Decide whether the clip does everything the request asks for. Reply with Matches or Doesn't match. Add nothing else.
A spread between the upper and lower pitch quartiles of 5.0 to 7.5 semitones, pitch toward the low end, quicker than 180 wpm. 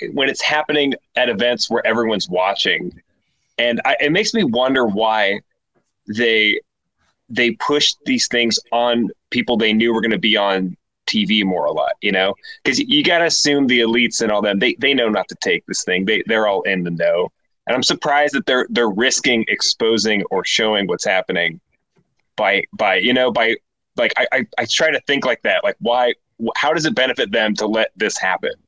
Matches